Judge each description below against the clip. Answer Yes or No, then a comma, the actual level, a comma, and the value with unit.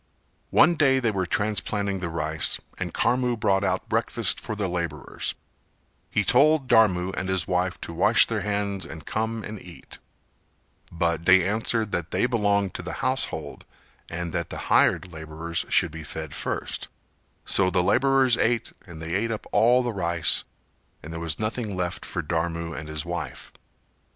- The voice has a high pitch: No, very low, 95 Hz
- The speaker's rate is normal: Yes, average, 170 wpm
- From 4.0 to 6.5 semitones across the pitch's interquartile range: Yes, average, 4.5 semitones